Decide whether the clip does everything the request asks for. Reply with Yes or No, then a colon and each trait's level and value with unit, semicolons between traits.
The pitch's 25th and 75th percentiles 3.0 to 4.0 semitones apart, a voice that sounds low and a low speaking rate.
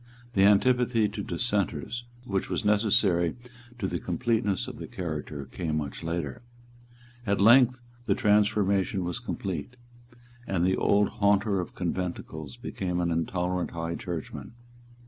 Yes: average, 3.5 semitones; very low, 95 Hz; slow, 130 wpm